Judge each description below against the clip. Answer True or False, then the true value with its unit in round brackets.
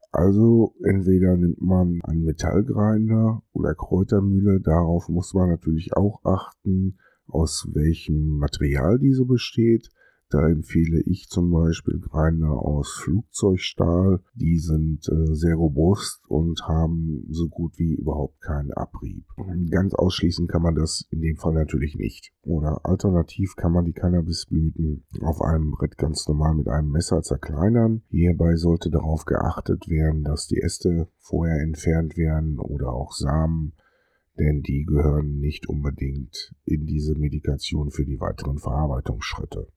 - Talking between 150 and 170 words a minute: False (135 wpm)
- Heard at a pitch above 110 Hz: False (80 Hz)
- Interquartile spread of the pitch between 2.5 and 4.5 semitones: True (3.1 semitones)